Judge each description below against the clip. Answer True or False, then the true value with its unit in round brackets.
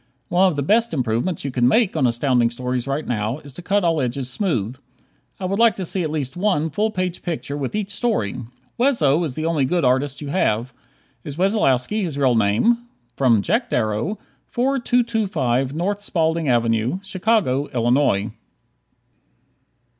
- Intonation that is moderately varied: False (7.5 semitones)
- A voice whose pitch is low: False (150 Hz)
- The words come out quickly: False (160 wpm)